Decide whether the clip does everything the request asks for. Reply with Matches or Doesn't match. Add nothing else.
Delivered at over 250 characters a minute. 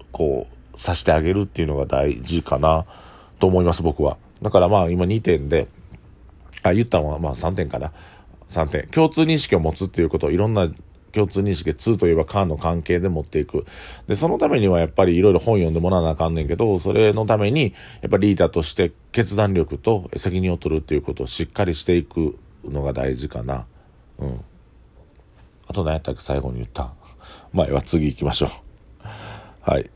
Matches